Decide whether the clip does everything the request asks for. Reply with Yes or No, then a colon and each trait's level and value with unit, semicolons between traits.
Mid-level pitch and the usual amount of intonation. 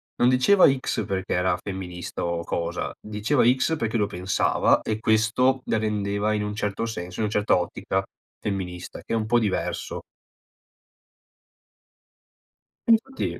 No: low, 105 Hz; average, 3.3 semitones